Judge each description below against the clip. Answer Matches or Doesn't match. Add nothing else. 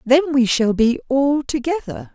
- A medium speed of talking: Matches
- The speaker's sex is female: Matches